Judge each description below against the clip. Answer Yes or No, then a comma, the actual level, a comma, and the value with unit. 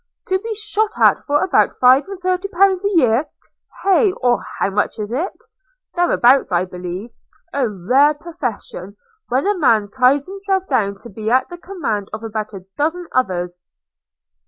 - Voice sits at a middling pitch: No, very high, 260 Hz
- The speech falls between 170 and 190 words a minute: Yes, average, 175 wpm